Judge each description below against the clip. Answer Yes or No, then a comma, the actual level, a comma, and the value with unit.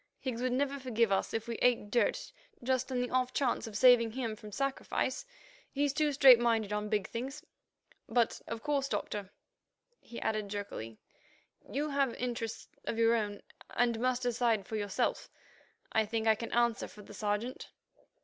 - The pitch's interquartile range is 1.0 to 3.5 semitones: Yes, average, 2.9 semitones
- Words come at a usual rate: Yes, average, 170 wpm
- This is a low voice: No, high, 235 Hz